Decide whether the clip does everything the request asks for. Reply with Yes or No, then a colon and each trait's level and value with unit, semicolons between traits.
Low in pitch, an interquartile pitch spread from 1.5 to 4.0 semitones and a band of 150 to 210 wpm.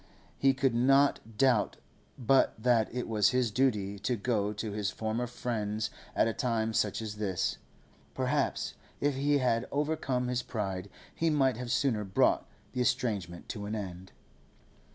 Yes: low, 115 Hz; average, 3.5 semitones; average, 155 wpm